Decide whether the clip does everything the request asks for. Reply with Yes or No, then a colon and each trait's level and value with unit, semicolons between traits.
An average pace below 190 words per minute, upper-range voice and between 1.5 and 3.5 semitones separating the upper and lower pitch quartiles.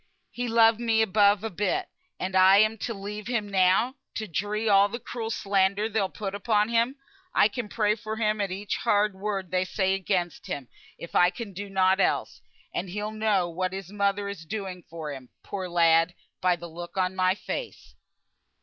No: average, 195 wpm; high, 200 Hz; narrow, 2.6 semitones